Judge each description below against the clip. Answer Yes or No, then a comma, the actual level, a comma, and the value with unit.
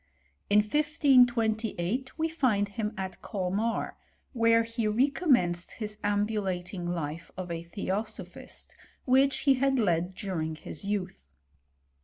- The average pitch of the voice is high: Yes, high, 210 Hz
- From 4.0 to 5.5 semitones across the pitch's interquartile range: Yes, average, 5.2 semitones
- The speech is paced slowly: Yes, slow, 120 wpm